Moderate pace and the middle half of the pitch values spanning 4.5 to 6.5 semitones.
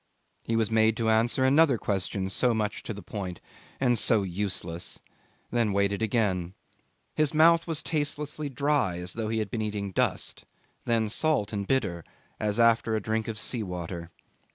No: average, 170 wpm; average, 3.6 semitones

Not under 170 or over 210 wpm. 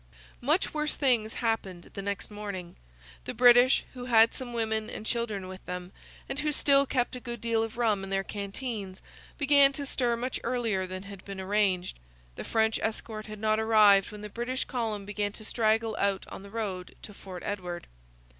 Yes: average, 190 wpm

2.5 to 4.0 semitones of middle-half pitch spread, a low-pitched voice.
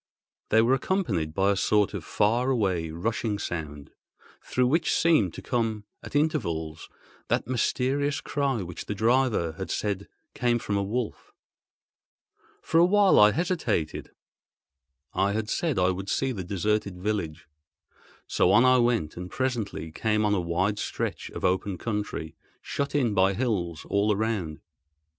No: wide, 5.5 semitones; low, 105 Hz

